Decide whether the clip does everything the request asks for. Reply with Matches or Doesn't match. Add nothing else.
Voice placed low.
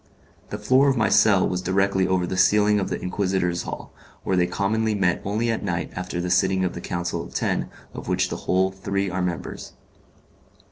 Matches